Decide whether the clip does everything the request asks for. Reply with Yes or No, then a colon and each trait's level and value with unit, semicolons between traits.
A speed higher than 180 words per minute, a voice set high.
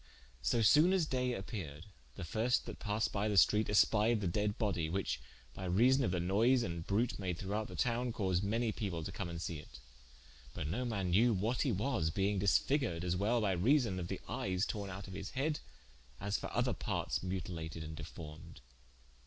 No: average, 200 wpm; low, 100 Hz